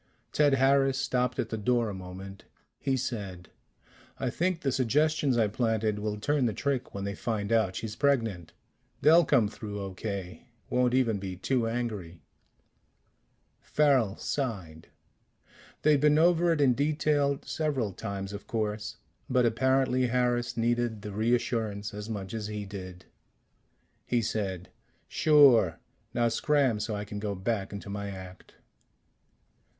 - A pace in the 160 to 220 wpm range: No, average, 145 wpm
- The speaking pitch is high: No, low, 115 Hz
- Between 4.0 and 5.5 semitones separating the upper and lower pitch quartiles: Yes, average, 4.5 semitones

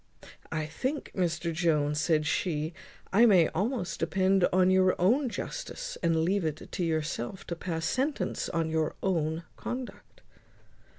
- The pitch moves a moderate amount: Yes, average, 3.4 semitones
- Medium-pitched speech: Yes, medium, 175 Hz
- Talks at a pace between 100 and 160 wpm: Yes, average, 140 wpm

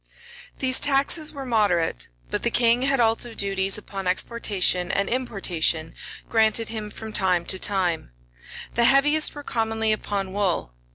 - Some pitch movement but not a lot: Yes, average, 4.0 semitones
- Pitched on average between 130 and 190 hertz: No, high, 215 Hz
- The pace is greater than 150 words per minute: No, average, 145 wpm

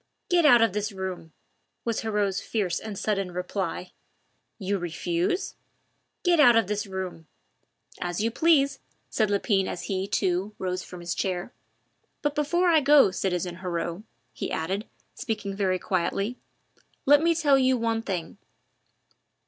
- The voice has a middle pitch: No, high, 200 Hz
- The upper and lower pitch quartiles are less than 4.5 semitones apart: No, wide, 5.4 semitones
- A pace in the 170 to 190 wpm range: No, average, 145 wpm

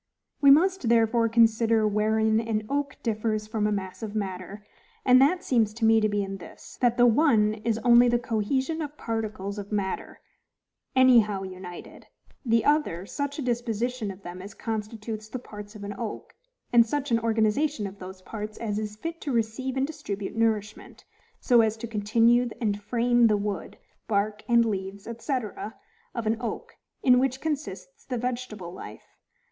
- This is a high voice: Yes, high, 225 Hz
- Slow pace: No, average, 175 wpm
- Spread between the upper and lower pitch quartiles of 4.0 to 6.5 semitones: No, average, 2.9 semitones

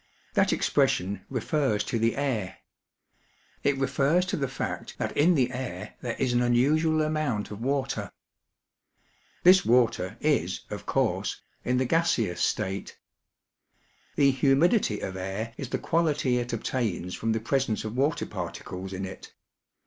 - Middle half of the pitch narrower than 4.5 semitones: No, average, 4.9 semitones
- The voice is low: Yes, low, 125 Hz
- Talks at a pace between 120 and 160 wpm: Yes, average, 150 wpm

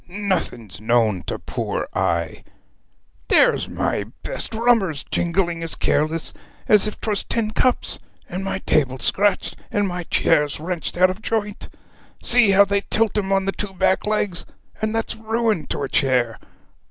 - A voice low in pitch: No, high, 190 Hz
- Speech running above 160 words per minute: No, average, 155 wpm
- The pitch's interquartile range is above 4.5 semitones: Yes, average, 5.3 semitones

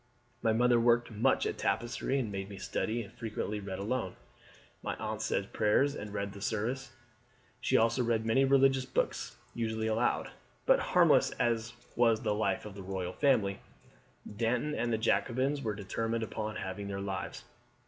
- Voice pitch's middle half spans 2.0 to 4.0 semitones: Yes, average, 2.9 semitones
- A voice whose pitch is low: Yes, low, 110 Hz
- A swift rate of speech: No, average, 170 wpm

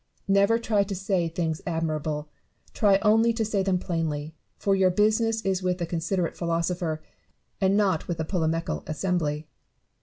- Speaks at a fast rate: No, average, 155 wpm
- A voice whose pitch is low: No, medium, 180 Hz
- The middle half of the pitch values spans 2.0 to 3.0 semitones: No, average, 3.5 semitones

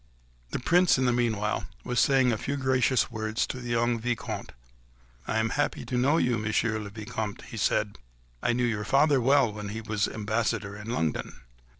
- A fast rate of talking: No, average, 190 wpm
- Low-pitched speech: Yes, low, 115 Hz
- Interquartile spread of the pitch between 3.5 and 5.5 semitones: No, average, 2.8 semitones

